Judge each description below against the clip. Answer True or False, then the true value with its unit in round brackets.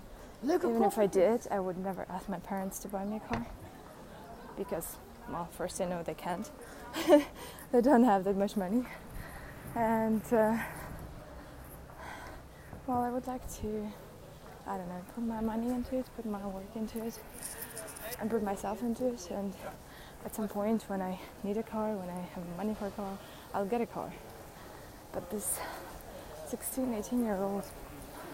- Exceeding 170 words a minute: False (165 wpm)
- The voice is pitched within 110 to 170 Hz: False (215 Hz)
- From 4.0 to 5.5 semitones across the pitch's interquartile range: False (3.0 semitones)